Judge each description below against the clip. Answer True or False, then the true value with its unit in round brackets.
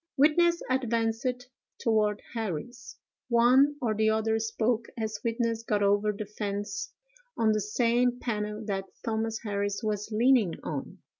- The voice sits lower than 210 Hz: False (225 Hz)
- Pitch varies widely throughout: False (2.4 semitones)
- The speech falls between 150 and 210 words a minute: False (135 wpm)